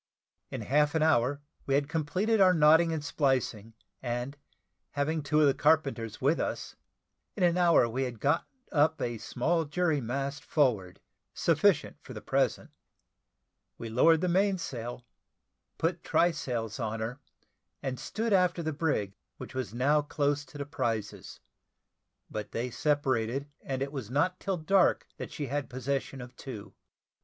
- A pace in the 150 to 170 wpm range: Yes, average, 155 wpm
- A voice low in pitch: No, medium, 145 Hz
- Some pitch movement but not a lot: Yes, average, 4.6 semitones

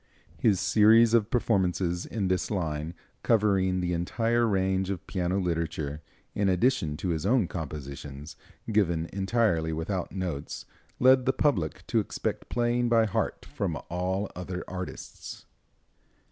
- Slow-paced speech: Yes, slow, 130 wpm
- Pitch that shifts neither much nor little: Yes, average, 4.5 semitones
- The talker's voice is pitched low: Yes, very low, 95 Hz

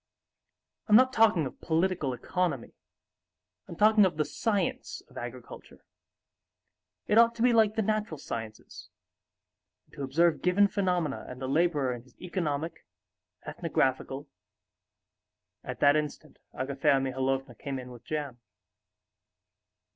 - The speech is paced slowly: Yes, slow, 125 wpm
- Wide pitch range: Yes, wide, 7.1 semitones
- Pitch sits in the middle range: Yes, medium, 155 Hz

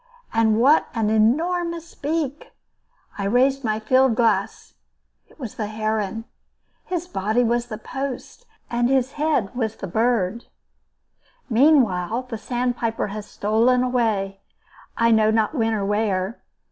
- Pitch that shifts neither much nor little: Yes, average, 3.3 semitones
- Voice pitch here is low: No, high, 230 Hz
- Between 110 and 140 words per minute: Yes, slow, 135 wpm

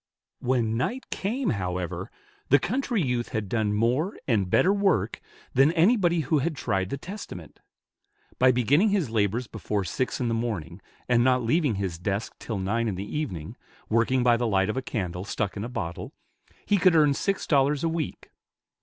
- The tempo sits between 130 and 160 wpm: No, average, 180 wpm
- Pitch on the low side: Yes, low, 120 Hz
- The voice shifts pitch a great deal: Yes, wide, 7.0 semitones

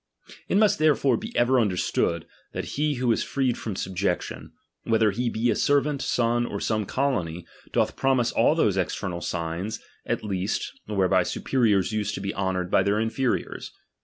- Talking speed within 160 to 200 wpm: Yes, average, 170 wpm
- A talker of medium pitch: No, low, 110 Hz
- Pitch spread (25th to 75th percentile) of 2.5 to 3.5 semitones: No, average, 5.3 semitones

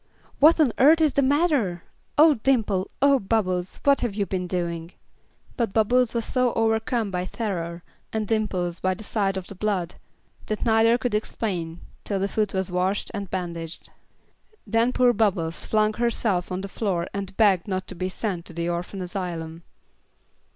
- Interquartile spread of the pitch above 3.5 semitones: Yes, average, 4.0 semitones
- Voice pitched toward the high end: Yes, high, 200 Hz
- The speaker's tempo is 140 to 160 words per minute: No, average, 170 wpm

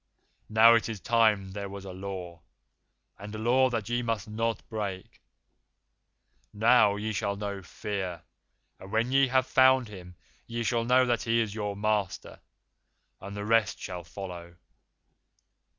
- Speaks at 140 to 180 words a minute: Yes, average, 150 wpm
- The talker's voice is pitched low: Yes, low, 105 Hz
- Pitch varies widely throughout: No, average, 2.8 semitones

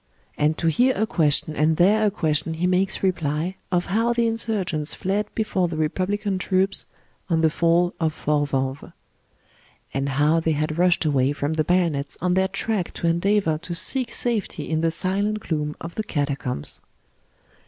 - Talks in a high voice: No, medium, 170 Hz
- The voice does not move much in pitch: No, average, 4.2 semitones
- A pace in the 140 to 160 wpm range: No, average, 175 wpm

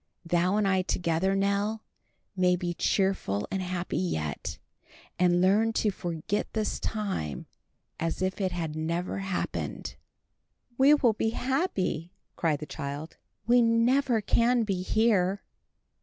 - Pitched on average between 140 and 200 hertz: Yes, high, 190 Hz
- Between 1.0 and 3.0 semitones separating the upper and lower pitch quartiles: No, average, 4.1 semitones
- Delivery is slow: Yes, slow, 130 wpm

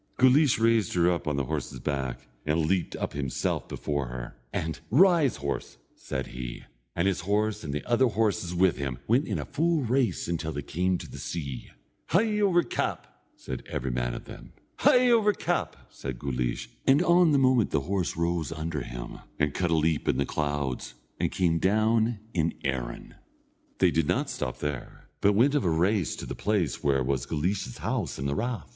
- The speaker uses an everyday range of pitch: No, wide, 8.6 semitones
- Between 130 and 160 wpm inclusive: No, average, 195 wpm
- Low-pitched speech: Yes, very low, 85 Hz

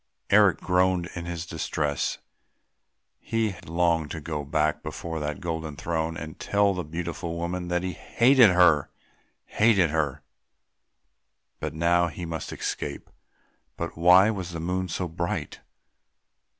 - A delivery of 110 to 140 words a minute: Yes, slow, 135 wpm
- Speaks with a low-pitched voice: Yes, very low, 85 Hz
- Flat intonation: Yes, narrow, 2.2 semitones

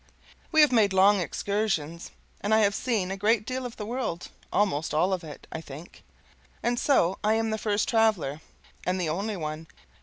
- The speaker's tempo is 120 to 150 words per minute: No, average, 190 wpm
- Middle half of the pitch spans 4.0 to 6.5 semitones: Yes, average, 4.6 semitones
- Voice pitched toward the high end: Yes, high, 200 Hz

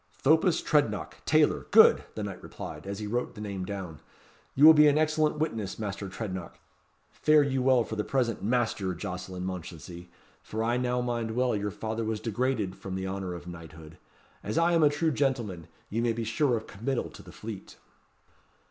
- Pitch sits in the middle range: No, low, 110 Hz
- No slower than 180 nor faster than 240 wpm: Yes, average, 190 wpm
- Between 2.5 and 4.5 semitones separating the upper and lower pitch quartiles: No, average, 5.2 semitones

